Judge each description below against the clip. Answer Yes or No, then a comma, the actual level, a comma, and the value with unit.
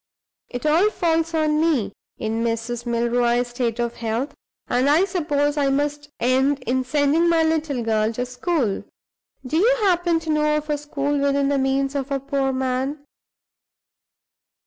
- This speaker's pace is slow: No, average, 160 wpm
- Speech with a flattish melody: No, average, 3.6 semitones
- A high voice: Yes, very high, 280 Hz